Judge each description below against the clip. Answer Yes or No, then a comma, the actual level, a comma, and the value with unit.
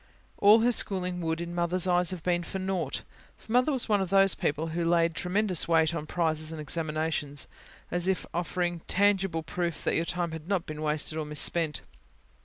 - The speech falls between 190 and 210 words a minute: Yes, average, 195 wpm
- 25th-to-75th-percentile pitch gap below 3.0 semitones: Yes, narrow, 2.6 semitones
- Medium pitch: Yes, medium, 170 Hz